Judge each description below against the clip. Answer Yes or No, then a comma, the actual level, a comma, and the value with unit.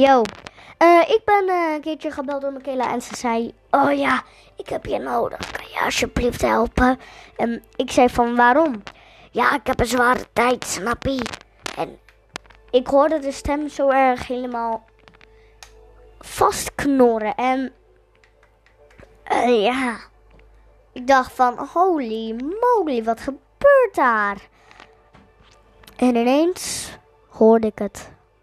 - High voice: Yes, very high, 255 Hz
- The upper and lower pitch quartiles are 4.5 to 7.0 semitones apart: No, average, 3.4 semitones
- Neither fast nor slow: No, slow, 130 wpm